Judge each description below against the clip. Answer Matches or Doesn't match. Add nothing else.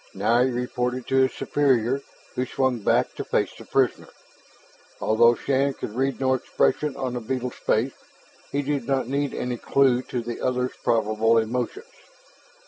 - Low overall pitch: Matches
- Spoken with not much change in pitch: Matches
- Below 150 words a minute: Doesn't match